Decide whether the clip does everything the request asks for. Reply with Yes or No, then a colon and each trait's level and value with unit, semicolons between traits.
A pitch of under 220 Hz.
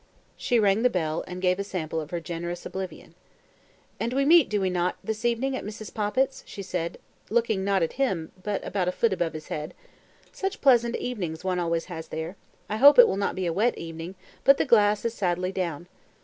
Yes: high, 190 Hz